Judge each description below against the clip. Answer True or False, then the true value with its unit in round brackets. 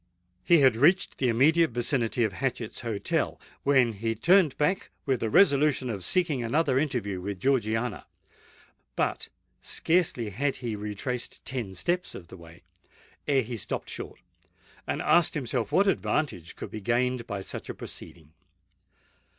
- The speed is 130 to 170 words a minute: True (150 wpm)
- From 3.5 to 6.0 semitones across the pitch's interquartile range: True (5.0 semitones)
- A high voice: False (125 Hz)